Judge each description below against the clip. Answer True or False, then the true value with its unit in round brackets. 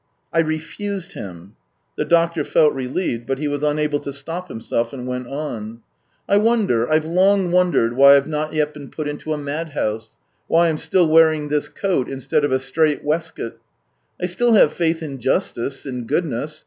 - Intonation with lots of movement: False (3.7 semitones)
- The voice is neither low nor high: True (150 Hz)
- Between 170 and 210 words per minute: True (190 wpm)